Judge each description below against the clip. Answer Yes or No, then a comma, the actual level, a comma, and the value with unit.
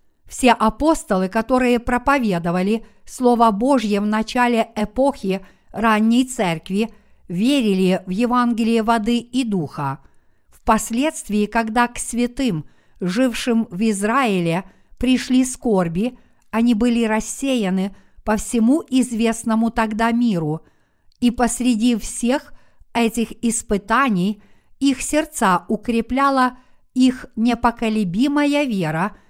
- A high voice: Yes, high, 230 Hz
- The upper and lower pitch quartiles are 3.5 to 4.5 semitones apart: No, average, 3.0 semitones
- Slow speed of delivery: Yes, slow, 90 wpm